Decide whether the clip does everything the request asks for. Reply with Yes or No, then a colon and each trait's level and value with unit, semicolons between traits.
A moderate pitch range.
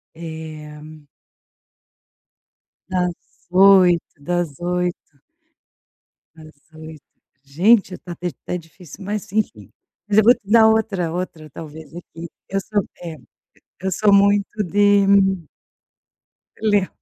Yes: average, 4.0 semitones